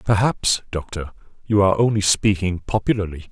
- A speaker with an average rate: No, slow, 125 wpm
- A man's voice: Yes, male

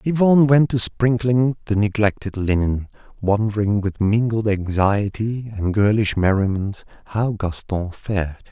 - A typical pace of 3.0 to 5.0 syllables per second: Yes, 4.4 syllables/s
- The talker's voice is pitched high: No, low, 105 Hz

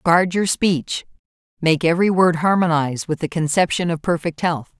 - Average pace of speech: Yes, average, 165 wpm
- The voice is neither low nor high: Yes, medium, 165 Hz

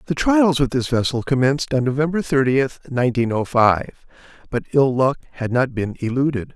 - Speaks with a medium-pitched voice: No, low, 130 Hz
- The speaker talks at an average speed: Yes, average, 175 wpm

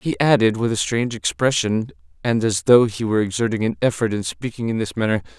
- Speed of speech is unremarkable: No, fast, 210 wpm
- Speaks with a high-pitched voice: No, low, 115 Hz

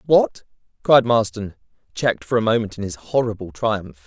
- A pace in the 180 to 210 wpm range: No, average, 160 wpm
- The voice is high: No, low, 110 Hz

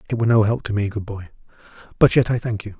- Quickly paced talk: Yes, fast, 280 wpm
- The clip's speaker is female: No, male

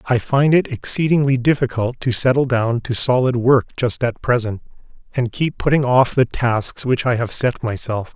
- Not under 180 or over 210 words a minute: Yes, average, 185 wpm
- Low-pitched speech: Yes, low, 125 Hz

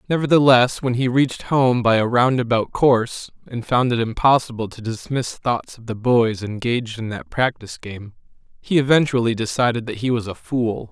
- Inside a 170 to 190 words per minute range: Yes, average, 175 wpm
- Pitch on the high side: No, low, 120 Hz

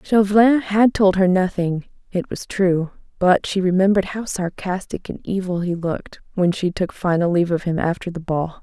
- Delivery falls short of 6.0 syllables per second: Yes, 5.1 syllables/s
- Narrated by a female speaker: Yes, female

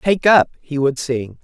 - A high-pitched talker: No, medium, 150 Hz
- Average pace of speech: No, fast, 210 wpm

